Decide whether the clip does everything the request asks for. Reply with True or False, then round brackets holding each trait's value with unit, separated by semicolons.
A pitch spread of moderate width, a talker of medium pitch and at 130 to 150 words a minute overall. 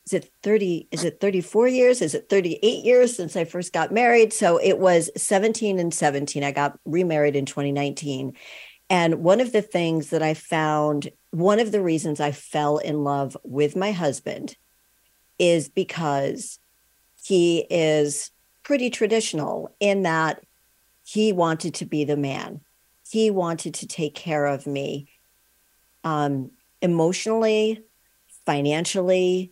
True (4.8 semitones; 165 Hz; 140 wpm)